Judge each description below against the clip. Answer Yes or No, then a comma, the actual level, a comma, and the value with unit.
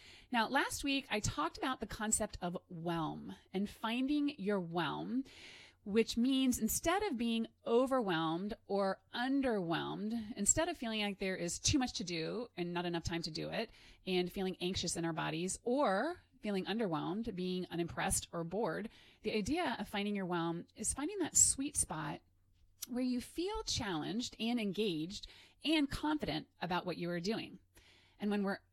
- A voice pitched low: No, high, 210 Hz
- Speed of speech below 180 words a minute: Yes, average, 165 wpm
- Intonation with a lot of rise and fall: Yes, wide, 6.0 semitones